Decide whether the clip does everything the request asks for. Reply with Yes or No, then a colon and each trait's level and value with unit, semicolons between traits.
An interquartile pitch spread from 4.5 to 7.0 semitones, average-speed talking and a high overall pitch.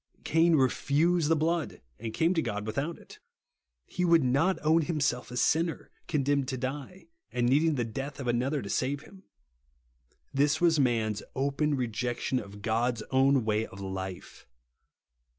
No: average, 4.8 semitones; average, 155 wpm; low, 135 Hz